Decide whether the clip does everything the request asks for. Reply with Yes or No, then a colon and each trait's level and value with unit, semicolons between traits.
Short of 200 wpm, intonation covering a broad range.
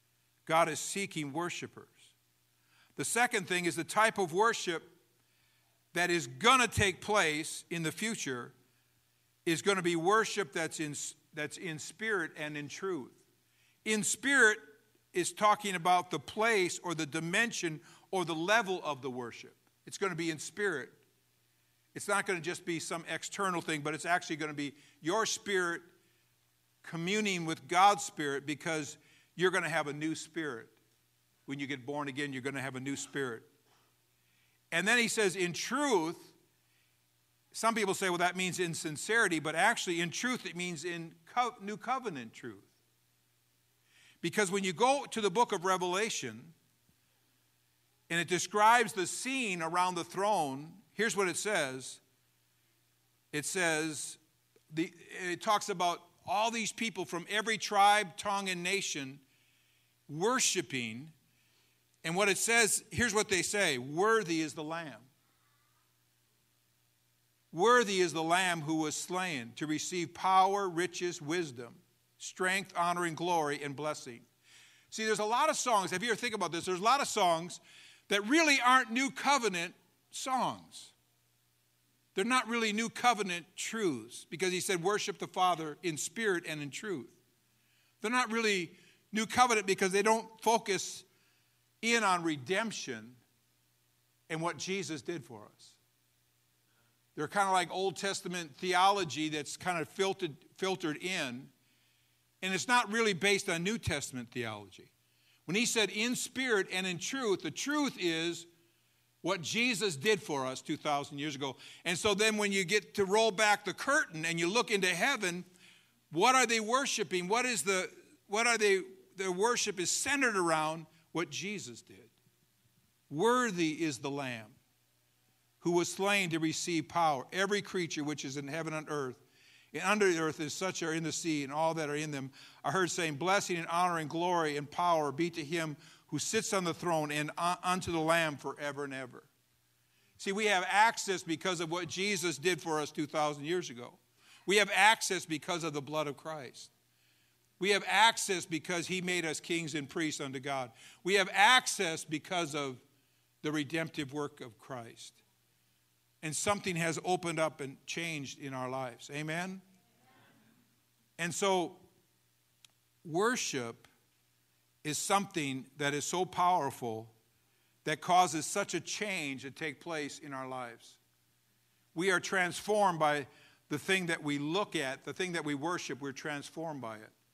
Yes: average, 160 wpm; wide, 5.8 semitones